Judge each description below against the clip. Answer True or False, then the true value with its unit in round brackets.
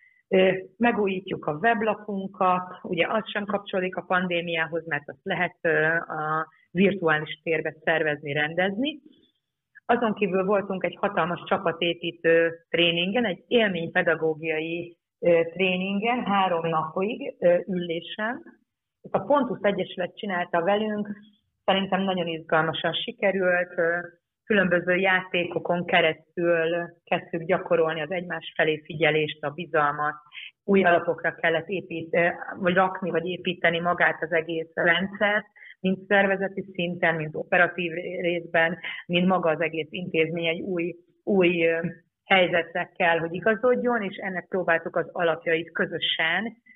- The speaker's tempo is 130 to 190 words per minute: False (110 wpm)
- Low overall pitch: False (175 Hz)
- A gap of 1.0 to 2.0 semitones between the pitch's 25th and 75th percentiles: False (2.6 semitones)